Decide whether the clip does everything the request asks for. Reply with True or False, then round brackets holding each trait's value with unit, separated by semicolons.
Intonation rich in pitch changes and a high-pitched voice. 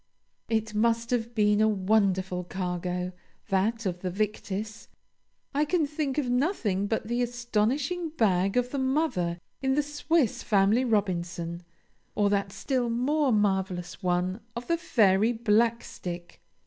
False (4.6 semitones; 215 Hz)